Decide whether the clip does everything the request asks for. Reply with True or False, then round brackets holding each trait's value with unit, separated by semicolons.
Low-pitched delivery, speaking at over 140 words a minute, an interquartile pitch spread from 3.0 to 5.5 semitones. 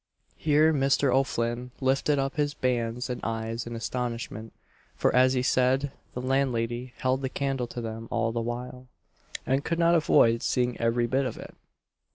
False (125 Hz; 170 wpm; 2.5 semitones)